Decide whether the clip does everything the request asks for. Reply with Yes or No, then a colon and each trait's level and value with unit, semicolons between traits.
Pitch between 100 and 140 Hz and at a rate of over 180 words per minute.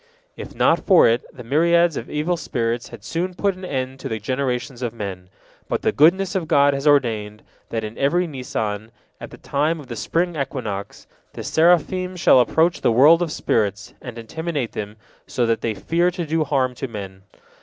Yes: low, 135 Hz; average, 195 wpm